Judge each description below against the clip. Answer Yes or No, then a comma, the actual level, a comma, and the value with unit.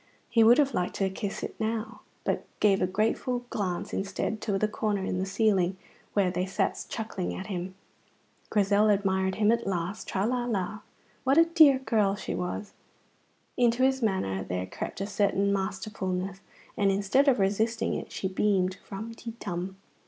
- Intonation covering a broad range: No, average, 2.9 semitones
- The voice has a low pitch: No, high, 200 Hz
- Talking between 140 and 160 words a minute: No, average, 175 wpm